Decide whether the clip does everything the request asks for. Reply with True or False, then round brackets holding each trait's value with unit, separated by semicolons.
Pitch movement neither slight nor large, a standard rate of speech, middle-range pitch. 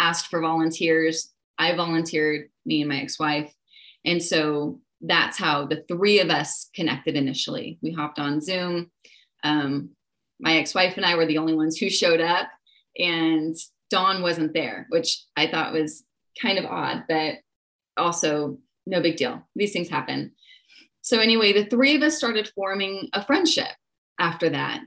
True (3.8 semitones; 165 wpm; 165 Hz)